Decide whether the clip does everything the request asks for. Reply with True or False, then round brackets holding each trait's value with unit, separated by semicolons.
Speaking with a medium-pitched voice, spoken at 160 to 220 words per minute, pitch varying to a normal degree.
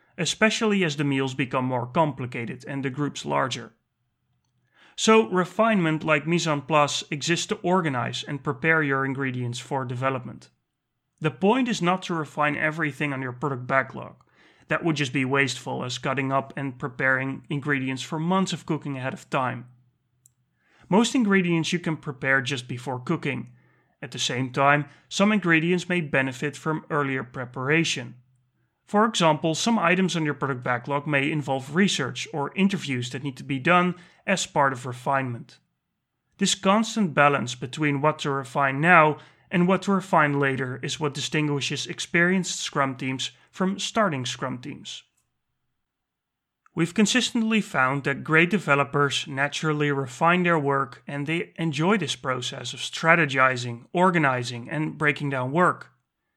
False (145 Hz; 150 wpm; 4.0 semitones)